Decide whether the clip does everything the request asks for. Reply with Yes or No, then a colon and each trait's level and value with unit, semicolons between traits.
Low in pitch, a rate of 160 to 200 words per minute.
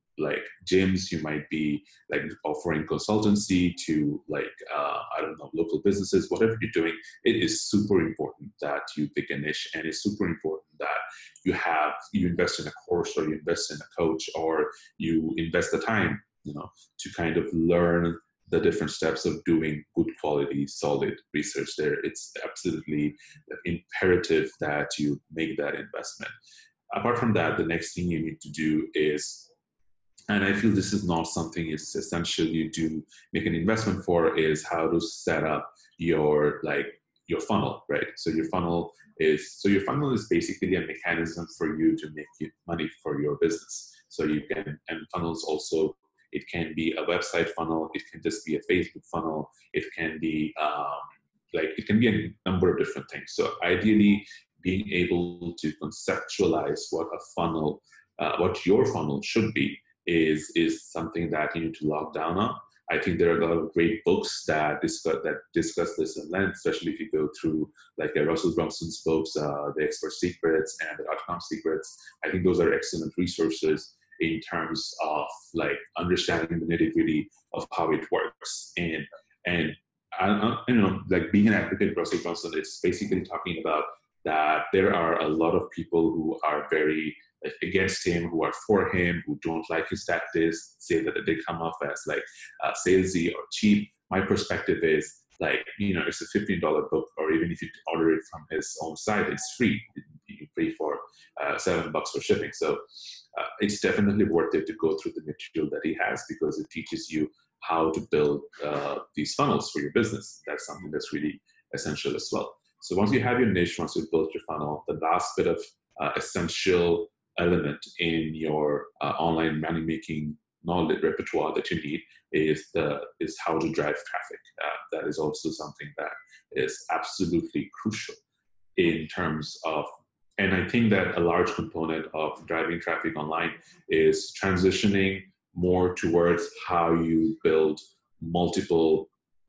Yes: very low, 90 Hz; average, 180 wpm